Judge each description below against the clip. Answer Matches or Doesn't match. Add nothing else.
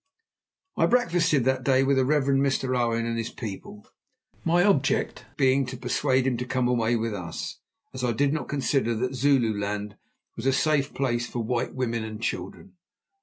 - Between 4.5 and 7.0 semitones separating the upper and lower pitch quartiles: Doesn't match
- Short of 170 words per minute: Doesn't match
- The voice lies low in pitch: Matches